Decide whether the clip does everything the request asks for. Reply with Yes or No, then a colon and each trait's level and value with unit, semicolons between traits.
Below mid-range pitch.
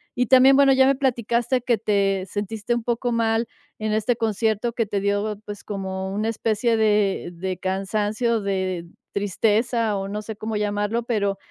No: high, 215 Hz